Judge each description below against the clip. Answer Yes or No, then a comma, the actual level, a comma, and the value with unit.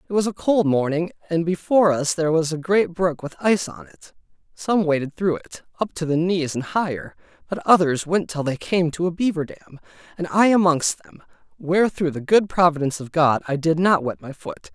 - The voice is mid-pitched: Yes, medium, 165 Hz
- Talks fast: Yes, fast, 220 wpm